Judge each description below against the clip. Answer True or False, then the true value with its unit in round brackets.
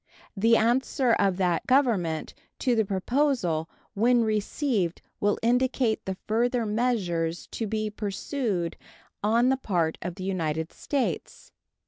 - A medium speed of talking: False (125 wpm)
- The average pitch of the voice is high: True (215 Hz)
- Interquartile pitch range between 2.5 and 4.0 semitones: False (5.2 semitones)